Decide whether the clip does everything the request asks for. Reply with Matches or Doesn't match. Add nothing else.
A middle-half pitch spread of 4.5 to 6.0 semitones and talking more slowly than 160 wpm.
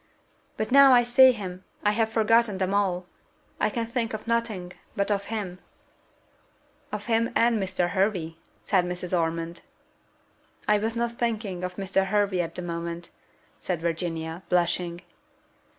Doesn't match